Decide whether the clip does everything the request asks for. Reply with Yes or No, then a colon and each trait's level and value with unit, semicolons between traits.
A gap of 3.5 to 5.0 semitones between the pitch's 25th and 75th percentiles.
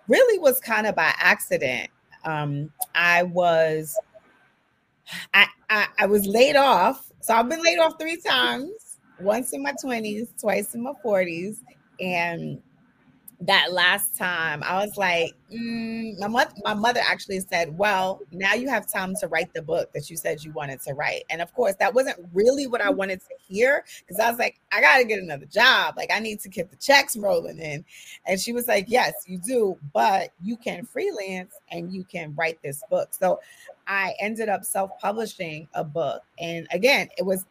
No: wide, 5.6 semitones